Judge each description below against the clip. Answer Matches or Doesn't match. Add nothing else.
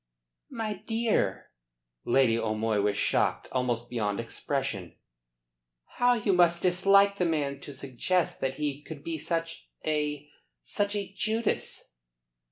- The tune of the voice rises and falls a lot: Matches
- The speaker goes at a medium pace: Doesn't match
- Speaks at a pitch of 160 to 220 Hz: Doesn't match